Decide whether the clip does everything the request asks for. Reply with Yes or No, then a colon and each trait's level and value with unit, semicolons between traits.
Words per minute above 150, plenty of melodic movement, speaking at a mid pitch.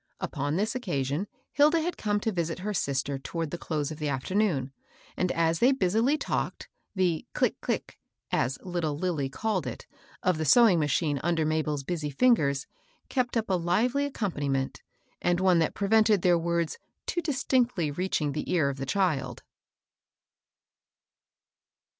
Yes: average, 160 wpm; wide, 6.3 semitones; medium, 175 Hz